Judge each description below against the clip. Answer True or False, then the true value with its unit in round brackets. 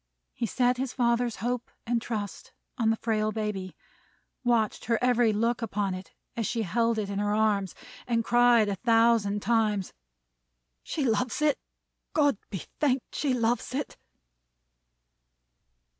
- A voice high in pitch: True (230 Hz)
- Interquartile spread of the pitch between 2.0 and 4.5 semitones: True (2.5 semitones)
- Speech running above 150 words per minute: False (145 wpm)